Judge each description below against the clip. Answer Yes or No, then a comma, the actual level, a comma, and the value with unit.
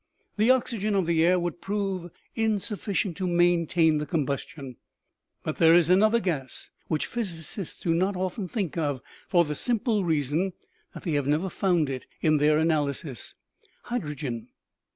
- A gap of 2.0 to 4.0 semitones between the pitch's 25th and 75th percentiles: No, average, 4.4 semitones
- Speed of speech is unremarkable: Yes, average, 155 wpm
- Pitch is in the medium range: Yes, medium, 170 Hz